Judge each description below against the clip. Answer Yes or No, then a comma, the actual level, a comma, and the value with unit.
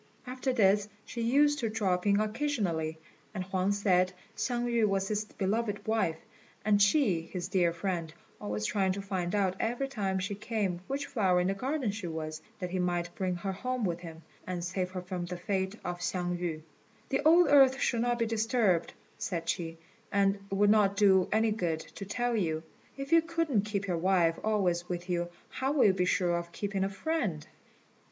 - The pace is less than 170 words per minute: No, average, 195 wpm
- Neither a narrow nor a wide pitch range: Yes, average, 4.0 semitones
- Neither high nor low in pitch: No, high, 195 Hz